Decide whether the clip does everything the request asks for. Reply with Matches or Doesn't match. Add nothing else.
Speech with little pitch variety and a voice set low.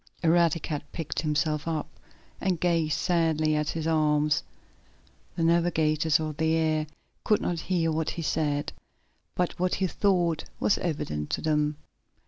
Doesn't match